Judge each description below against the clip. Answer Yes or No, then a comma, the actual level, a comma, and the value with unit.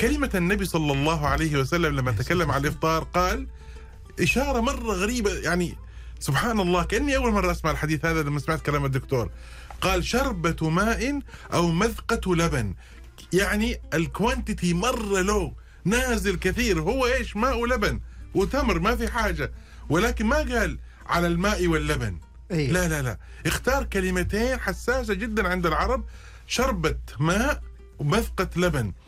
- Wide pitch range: Yes, wide, 7.3 semitones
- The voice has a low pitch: No, medium, 175 Hz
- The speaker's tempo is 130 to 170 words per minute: Yes, fast, 135 wpm